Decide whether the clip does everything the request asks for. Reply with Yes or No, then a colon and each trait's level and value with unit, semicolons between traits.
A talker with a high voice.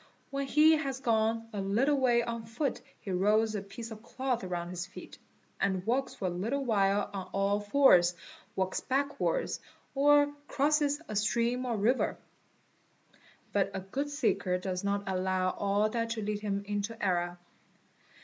Yes: high, 215 Hz